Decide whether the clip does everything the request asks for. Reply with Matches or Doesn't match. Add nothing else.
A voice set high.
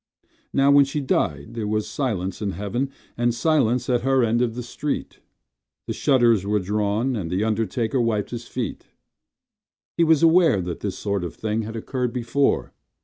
Doesn't match